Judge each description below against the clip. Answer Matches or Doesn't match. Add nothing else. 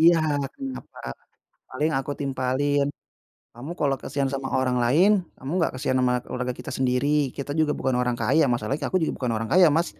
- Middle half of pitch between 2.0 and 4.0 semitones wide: Matches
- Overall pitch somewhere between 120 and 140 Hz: Matches